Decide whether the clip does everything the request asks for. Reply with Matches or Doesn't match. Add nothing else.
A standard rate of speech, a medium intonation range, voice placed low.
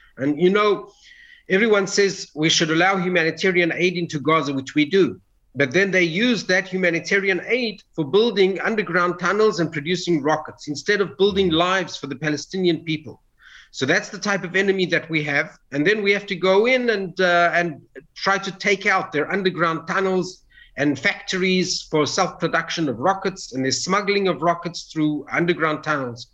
Doesn't match